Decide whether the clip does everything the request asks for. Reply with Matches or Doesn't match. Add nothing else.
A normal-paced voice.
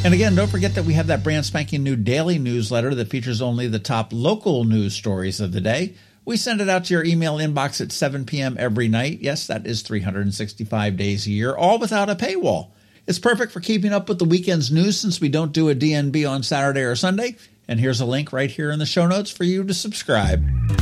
Doesn't match